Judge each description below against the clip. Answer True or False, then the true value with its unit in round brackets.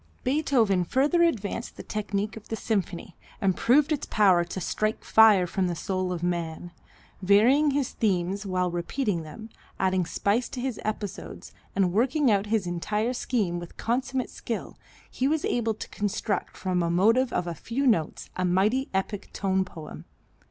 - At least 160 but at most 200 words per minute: True (165 wpm)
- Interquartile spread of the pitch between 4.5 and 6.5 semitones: True (4.9 semitones)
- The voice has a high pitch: True (205 Hz)